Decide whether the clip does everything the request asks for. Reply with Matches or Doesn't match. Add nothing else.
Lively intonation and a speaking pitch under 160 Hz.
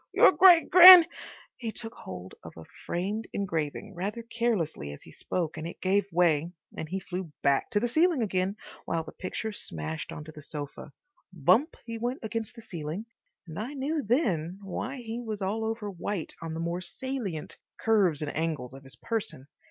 Doesn't match